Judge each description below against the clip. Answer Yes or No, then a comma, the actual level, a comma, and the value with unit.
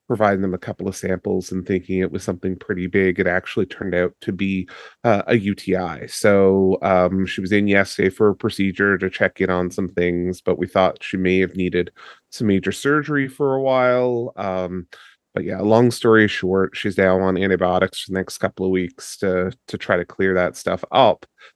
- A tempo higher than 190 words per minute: Yes, fast, 205 wpm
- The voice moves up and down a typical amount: No, narrow, 1.7 semitones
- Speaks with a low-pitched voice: Yes, very low, 95 Hz